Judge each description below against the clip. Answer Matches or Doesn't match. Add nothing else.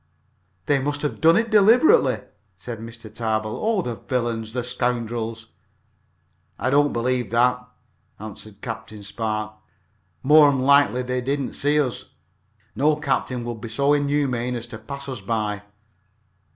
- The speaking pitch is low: Matches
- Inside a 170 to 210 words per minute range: Doesn't match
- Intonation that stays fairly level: Doesn't match